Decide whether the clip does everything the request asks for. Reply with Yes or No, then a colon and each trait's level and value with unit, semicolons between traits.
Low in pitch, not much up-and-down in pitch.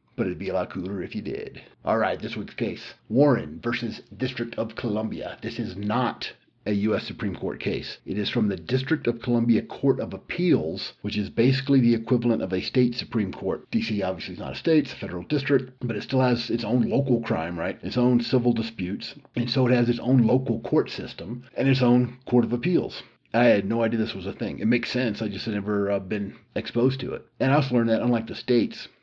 Yes: low, 120 Hz; narrow, 2.1 semitones